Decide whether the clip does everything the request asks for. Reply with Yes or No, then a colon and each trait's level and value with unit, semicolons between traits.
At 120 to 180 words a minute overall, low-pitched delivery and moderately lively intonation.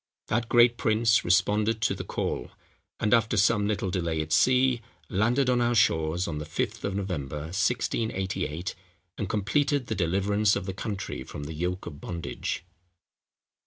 Yes: average, 160 wpm; low, 100 Hz; average, 4.7 semitones